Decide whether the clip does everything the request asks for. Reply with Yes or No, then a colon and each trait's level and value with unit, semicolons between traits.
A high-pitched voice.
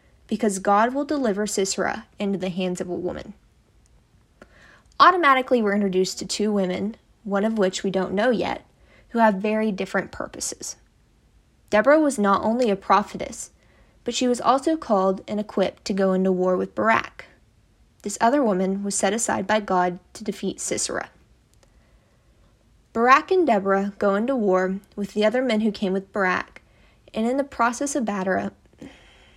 Yes: high, 205 Hz